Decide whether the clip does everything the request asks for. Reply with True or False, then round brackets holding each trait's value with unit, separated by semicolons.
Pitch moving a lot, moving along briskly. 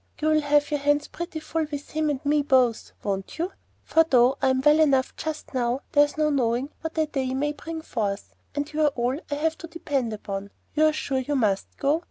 False (3.0 semitones; 210 wpm)